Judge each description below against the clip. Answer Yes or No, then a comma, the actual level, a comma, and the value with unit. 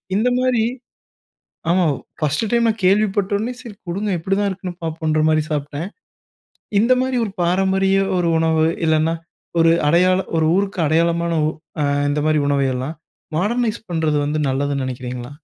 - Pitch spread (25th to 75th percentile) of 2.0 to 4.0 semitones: No, average, 4.6 semitones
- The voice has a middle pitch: Yes, medium, 170 Hz